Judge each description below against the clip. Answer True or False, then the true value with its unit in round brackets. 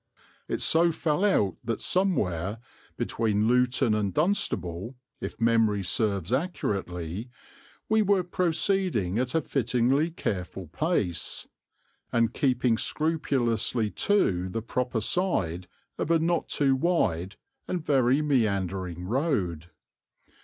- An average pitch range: False (8.5 semitones)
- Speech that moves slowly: True (110 wpm)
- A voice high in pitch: False (120 Hz)